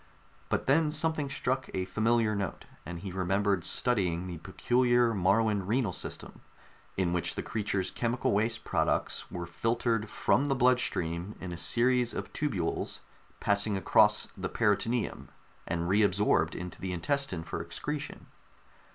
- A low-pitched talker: Yes, low, 105 Hz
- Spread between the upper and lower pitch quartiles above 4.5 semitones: Yes, average, 4.9 semitones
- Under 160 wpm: Yes, average, 145 wpm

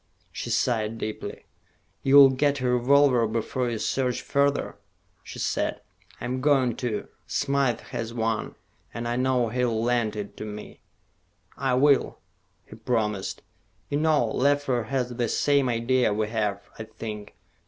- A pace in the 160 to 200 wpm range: No, average, 145 wpm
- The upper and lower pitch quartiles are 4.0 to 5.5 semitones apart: No, average, 3.2 semitones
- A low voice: Yes, low, 120 Hz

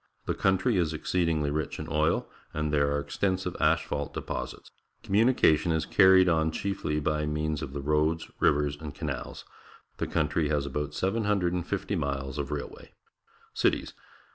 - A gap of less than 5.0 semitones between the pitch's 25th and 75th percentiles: Yes, average, 3.4 semitones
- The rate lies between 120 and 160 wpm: Yes, average, 145 wpm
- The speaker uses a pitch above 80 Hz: No, very low, 75 Hz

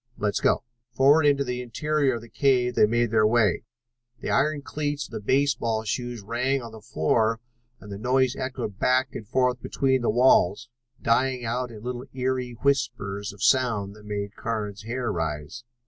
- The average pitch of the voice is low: Yes, low, 120 Hz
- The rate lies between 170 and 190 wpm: Yes, average, 180 wpm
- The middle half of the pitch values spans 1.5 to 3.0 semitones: No, average, 3.5 semitones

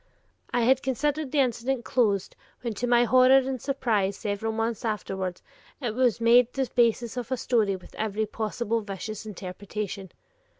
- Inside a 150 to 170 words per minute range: Yes, average, 160 wpm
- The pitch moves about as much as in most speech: Yes, average, 3.3 semitones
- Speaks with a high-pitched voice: Yes, high, 230 Hz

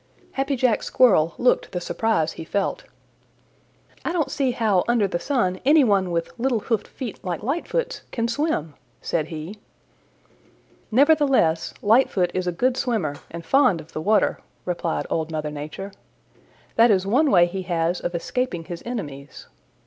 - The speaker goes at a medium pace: Yes, average, 155 wpm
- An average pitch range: No, wide, 7.0 semitones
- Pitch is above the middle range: Yes, high, 200 Hz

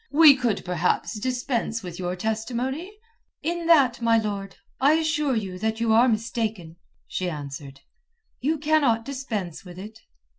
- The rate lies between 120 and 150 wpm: Yes, average, 145 wpm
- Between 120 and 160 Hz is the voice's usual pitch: No, high, 225 Hz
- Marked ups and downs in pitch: Yes, wide, 5.9 semitones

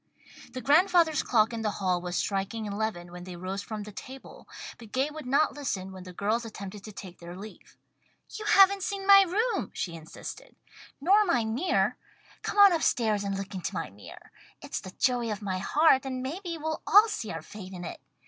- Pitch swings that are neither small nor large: No, wide, 8.6 semitones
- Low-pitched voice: No, high, 225 Hz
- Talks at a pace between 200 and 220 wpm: Yes, fast, 205 wpm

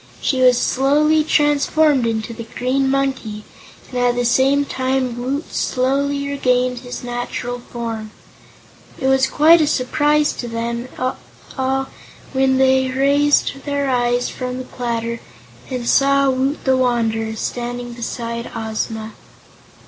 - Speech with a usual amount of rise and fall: No, narrow, 2.3 semitones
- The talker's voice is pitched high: Yes, very high, 255 Hz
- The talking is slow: Yes, slow, 130 wpm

